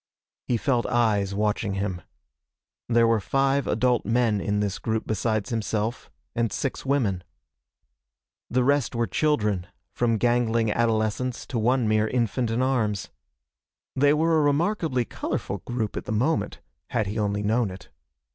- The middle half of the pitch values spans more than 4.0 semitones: No, average, 3.2 semitones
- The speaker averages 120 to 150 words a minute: Yes, average, 145 wpm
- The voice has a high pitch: No, low, 115 Hz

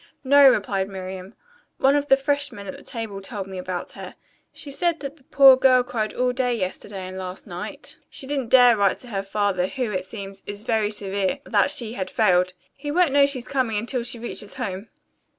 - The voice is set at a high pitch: Yes, high, 225 Hz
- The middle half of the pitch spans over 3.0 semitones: Yes, wide, 5.4 semitones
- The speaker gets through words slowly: No, fast, 205 wpm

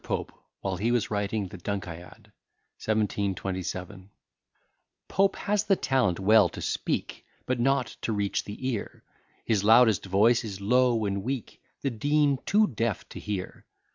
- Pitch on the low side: Yes, low, 110 Hz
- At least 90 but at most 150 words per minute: Yes, average, 145 wpm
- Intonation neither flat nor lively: Yes, average, 4.3 semitones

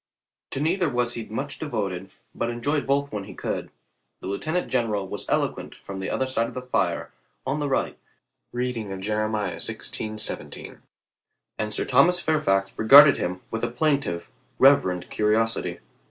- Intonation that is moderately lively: Yes, average, 5.0 semitones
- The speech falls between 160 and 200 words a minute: Yes, average, 165 wpm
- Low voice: Yes, low, 120 Hz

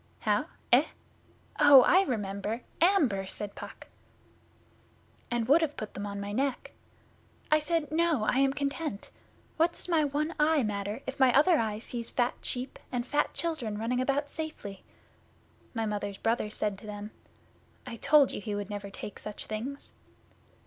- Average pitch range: No, wide, 6.0 semitones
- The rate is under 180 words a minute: Yes, average, 165 wpm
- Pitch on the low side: No, high, 245 Hz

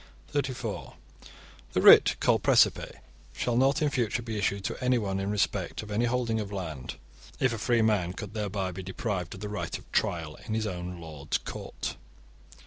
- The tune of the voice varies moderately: Yes, average, 4.0 semitones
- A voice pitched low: Yes, low, 105 Hz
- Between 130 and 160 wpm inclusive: No, average, 180 wpm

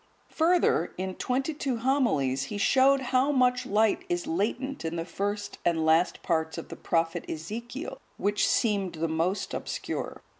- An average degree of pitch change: No, wide, 7.6 semitones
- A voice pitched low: No, high, 205 Hz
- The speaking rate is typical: Yes, average, 155 wpm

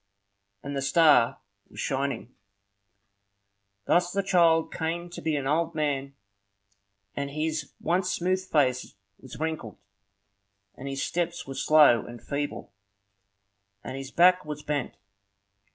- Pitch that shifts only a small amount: No, average, 3.7 semitones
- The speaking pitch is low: No, medium, 150 Hz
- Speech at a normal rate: No, slow, 125 wpm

